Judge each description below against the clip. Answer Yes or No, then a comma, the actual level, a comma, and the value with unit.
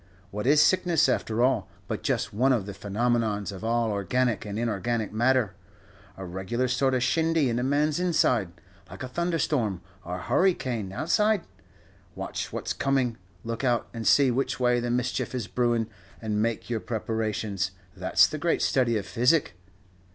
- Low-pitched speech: Yes, low, 120 Hz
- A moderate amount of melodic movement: Yes, average, 3.8 semitones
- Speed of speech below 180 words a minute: Yes, average, 170 wpm